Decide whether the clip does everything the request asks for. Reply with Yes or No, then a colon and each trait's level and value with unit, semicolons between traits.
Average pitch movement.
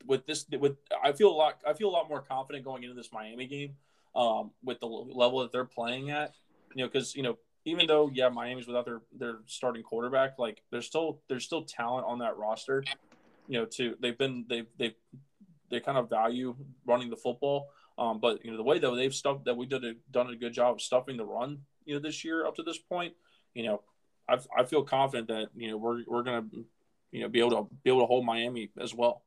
Yes: average, 3.0 semitones